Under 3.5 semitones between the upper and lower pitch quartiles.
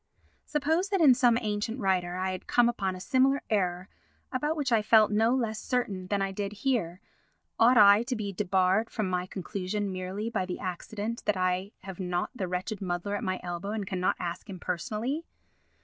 No: average, 4.0 semitones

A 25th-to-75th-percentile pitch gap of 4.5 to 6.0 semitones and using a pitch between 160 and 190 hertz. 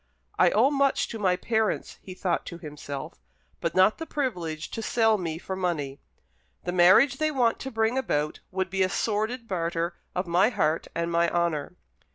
Yes: average, 5.0 semitones; medium, 185 Hz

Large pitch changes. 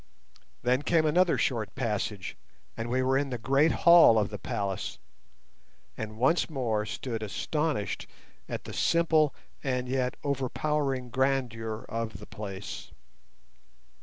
No: average, 4.2 semitones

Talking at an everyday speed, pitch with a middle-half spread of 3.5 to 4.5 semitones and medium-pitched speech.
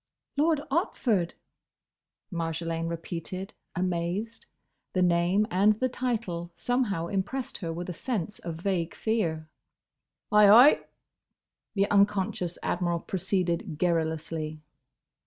No: slow, 100 wpm; average, 3.9 semitones; medium, 180 Hz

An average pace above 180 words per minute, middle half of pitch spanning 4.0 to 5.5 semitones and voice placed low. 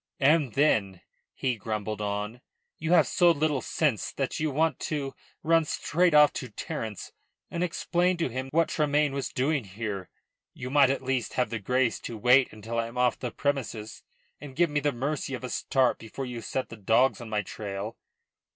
Yes: average, 190 wpm; average, 4.9 semitones; low, 130 Hz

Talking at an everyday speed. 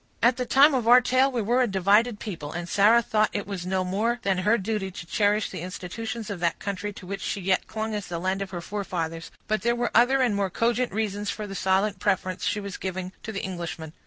No: fast, 245 wpm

